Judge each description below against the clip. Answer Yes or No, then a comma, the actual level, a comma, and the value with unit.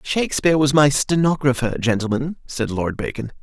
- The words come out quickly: No, average, 140 wpm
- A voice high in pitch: No, medium, 140 Hz